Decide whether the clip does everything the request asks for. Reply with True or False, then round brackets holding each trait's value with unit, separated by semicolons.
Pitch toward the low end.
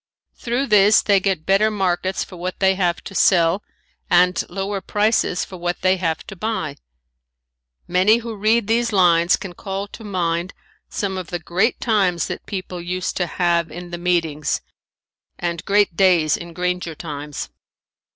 False (185 Hz)